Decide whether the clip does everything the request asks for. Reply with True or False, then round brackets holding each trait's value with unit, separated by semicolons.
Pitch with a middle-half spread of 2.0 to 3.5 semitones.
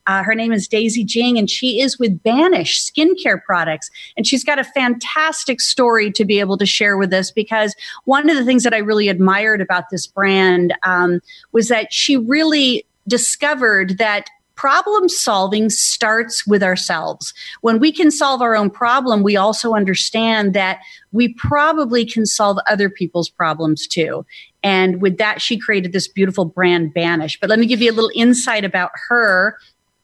False (4.3 semitones)